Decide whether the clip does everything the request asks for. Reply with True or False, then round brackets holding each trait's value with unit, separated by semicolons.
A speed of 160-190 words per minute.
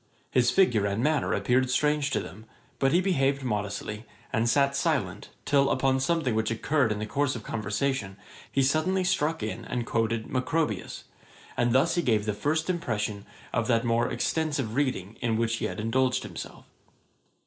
True (170 wpm)